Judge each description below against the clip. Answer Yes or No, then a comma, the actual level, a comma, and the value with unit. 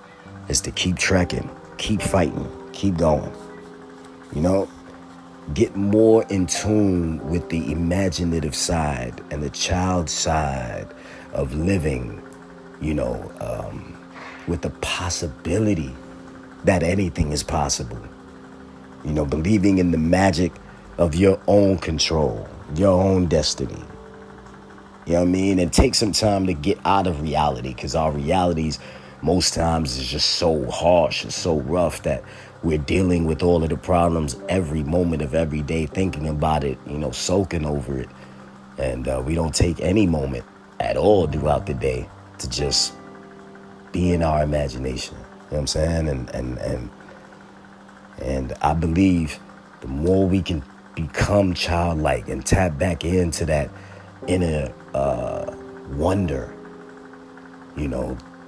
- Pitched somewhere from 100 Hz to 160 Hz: No, very low, 85 Hz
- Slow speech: No, average, 145 wpm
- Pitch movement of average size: Yes, average, 4.1 semitones